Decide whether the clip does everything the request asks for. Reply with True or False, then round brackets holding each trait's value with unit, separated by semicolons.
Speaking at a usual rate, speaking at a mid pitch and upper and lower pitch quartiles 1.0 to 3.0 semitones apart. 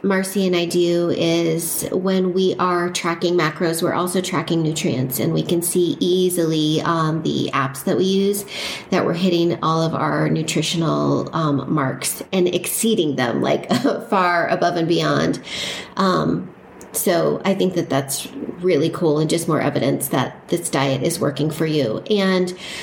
True (165 wpm; 170 Hz; 2.5 semitones)